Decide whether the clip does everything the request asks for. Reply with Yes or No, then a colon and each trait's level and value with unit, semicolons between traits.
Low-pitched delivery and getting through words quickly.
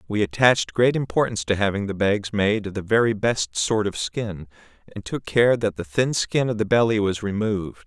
Yes: low, 105 Hz; fast, 215 wpm